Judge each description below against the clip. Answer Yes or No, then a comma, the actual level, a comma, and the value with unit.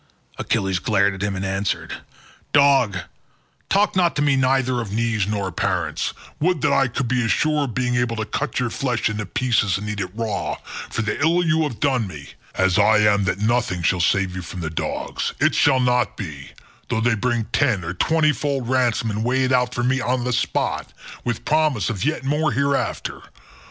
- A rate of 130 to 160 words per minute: No, average, 200 wpm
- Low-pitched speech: Yes, low, 120 Hz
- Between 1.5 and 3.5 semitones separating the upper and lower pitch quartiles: No, average, 4.8 semitones